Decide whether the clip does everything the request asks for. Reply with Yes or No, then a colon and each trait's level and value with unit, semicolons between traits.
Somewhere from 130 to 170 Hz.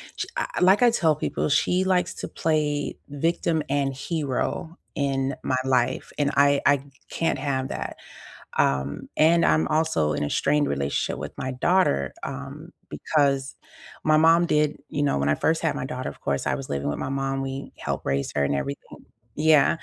Yes: medium, 140 Hz